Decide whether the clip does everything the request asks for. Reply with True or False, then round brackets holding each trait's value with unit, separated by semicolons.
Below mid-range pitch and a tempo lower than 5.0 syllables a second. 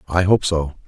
True (85 Hz; 4.8 syllables/s)